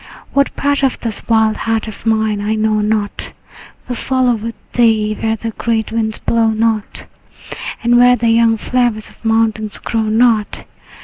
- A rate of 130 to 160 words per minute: No, average, 170 wpm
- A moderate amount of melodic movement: No, narrow, 1.2 semitones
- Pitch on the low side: No, high, 225 Hz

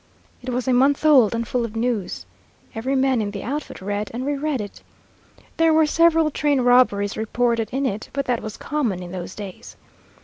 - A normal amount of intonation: Yes, average, 4.7 semitones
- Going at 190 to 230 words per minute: Yes, average, 195 wpm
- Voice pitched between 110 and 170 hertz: No, high, 245 Hz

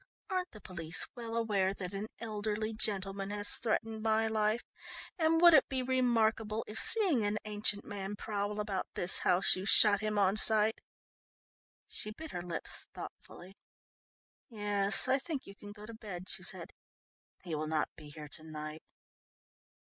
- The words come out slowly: No, average, 165 wpm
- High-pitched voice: Yes, high, 210 Hz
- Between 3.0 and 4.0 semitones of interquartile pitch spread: No, narrow, 2.6 semitones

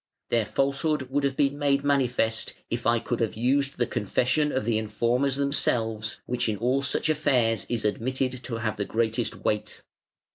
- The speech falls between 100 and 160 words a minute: No, average, 175 wpm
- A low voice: Yes, low, 125 Hz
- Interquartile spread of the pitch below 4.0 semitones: Yes, average, 3.5 semitones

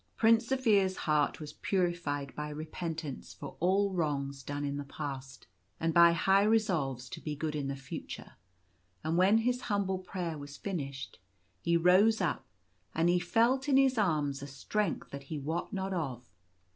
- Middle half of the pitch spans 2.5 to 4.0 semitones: No, wide, 5.4 semitones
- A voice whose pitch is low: No, medium, 170 Hz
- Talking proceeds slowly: No, average, 170 wpm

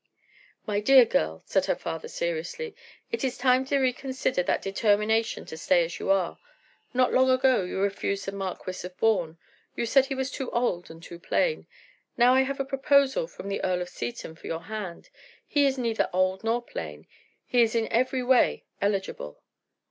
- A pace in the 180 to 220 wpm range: Yes, average, 185 wpm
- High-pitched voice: Yes, high, 225 Hz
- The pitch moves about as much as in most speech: No, wide, 6.1 semitones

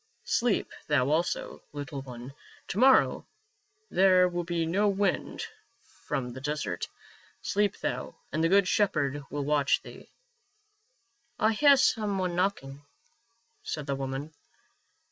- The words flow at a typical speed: No, slow, 130 wpm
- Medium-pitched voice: Yes, medium, 175 Hz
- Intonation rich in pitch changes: Yes, wide, 6.4 semitones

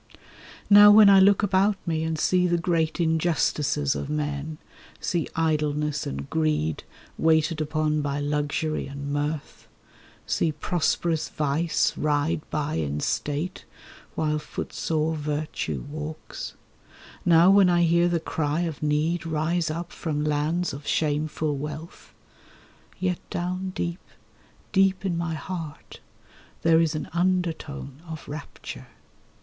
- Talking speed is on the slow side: Yes, slow, 125 wpm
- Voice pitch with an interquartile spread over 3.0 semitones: No, narrow, 2.5 semitones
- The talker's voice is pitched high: No, medium, 155 Hz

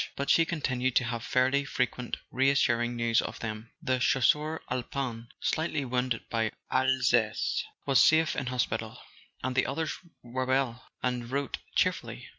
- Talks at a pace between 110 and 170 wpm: Yes, average, 150 wpm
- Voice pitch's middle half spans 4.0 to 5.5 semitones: No, narrow, 2.4 semitones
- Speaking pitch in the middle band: No, low, 130 Hz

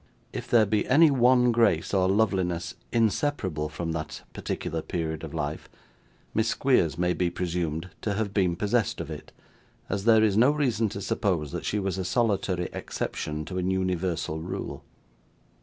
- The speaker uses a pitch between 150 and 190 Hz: No, very low, 95 Hz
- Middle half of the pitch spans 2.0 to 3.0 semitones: No, average, 4.5 semitones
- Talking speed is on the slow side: No, average, 165 wpm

